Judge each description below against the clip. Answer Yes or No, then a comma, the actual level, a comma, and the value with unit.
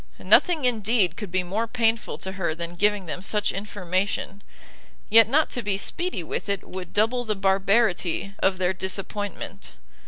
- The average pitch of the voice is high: Yes, high, 200 Hz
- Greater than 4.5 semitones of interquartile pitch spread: No, average, 3.0 semitones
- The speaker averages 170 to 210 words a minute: No, average, 160 wpm